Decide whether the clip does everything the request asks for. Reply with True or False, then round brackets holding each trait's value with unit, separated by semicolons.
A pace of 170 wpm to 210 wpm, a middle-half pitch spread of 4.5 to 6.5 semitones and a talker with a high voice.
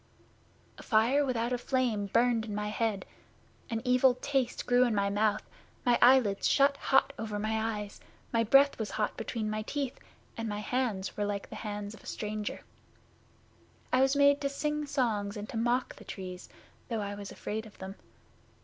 False (185 wpm; 3.4 semitones; 225 Hz)